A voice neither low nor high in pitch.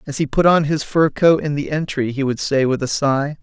Yes: medium, 145 Hz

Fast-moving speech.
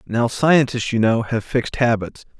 No: average, 175 wpm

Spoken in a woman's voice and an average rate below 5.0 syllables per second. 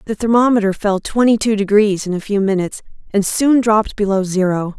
No: female; 5.8 syllables/s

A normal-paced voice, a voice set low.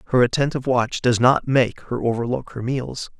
Yes: average, 190 wpm; low, 125 Hz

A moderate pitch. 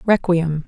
Yes: medium, 175 Hz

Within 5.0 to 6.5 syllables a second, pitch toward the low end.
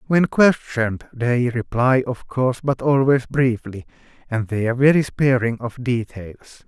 No: 4.6 syllables/s; low, 125 Hz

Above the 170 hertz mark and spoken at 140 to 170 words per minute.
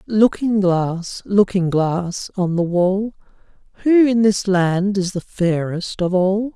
Yes: high, 190 Hz; average, 145 wpm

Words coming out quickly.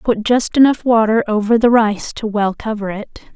No: average, 195 wpm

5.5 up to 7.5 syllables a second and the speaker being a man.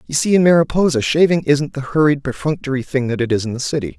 Yes: 6.5 syllables/s; male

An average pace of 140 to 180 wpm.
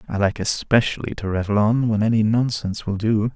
No: average, 195 wpm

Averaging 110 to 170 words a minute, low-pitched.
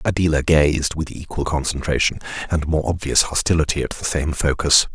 Yes: average, 160 wpm; very low, 75 Hz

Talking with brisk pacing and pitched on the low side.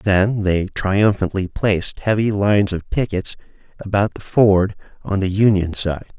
No: average, 145 wpm; low, 100 Hz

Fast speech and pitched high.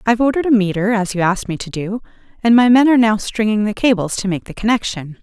Yes: fast, 255 wpm; high, 215 Hz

